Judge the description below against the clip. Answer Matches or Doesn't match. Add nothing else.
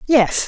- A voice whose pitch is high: Matches